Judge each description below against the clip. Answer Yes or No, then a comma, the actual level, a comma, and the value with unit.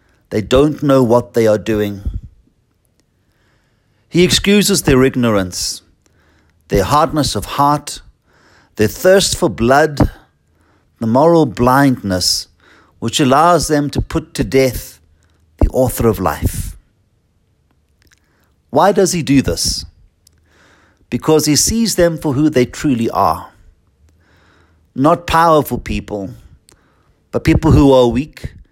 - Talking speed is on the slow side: Yes, slow, 115 wpm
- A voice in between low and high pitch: No, low, 110 Hz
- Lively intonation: Yes, wide, 8.3 semitones